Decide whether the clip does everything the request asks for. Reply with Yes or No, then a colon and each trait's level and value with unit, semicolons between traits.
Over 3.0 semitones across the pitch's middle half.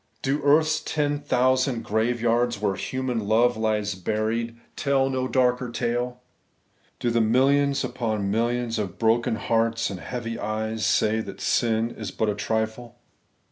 No: narrow, 2.5 semitones